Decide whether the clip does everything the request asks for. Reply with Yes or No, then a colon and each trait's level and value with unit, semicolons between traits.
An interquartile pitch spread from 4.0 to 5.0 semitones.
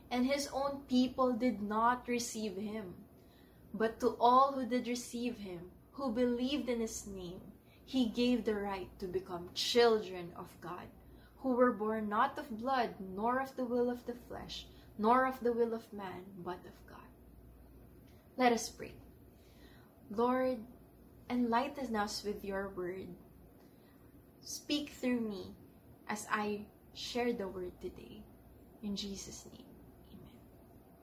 No: average, 3.6 semitones